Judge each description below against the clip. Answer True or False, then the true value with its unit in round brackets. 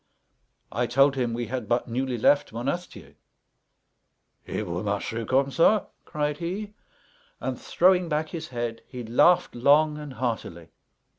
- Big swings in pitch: False (4.7 semitones)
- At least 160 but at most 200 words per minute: False (140 wpm)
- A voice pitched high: False (135 Hz)